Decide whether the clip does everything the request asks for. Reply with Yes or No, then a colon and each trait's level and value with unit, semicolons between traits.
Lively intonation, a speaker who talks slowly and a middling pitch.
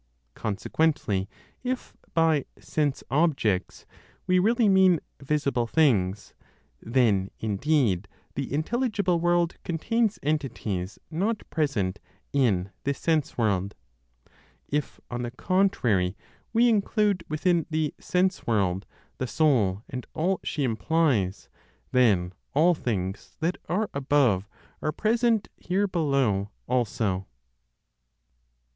Yes: wide, 8.6 semitones; slow, 105 wpm; medium, 145 Hz